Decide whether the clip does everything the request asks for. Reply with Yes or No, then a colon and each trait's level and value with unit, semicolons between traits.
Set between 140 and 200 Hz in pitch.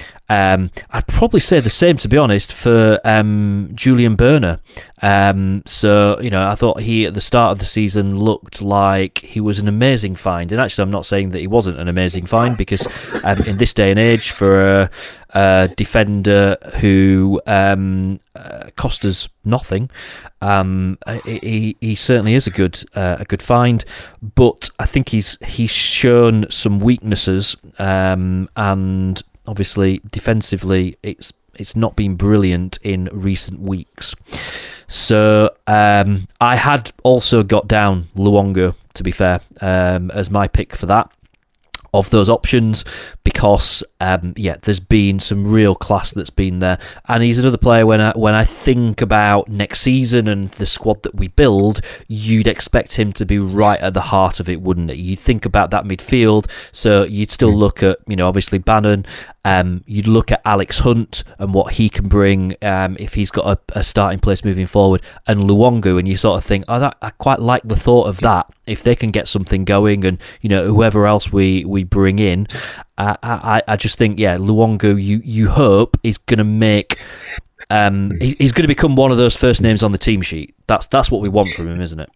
No: low, 100 Hz